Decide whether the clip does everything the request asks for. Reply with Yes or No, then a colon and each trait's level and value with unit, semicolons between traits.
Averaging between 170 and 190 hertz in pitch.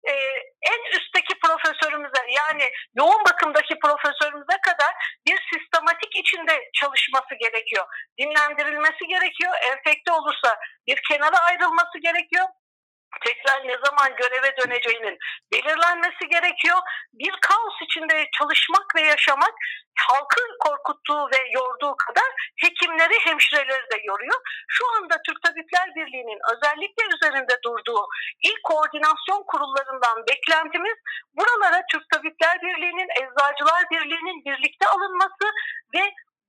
No: very high, 325 Hz